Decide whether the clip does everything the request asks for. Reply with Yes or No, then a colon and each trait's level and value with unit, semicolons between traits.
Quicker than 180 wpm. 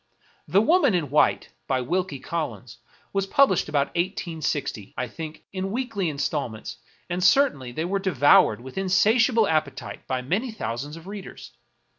No: average, 155 wpm